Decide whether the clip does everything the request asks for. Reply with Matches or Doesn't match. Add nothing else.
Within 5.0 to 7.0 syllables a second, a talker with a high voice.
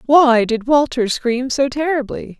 Doesn't match